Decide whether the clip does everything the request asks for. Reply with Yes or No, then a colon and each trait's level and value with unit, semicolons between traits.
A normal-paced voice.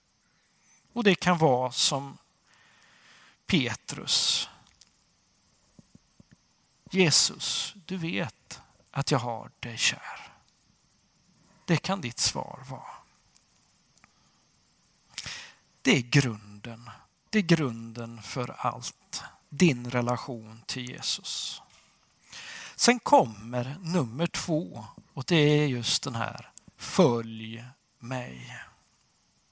No: slow, 85 wpm